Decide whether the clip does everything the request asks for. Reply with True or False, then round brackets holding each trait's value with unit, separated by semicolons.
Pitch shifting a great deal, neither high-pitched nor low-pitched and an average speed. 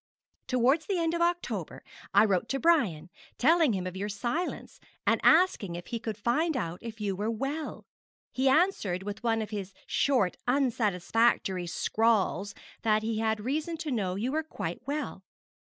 False (6.7 semitones; 230 Hz; 170 wpm)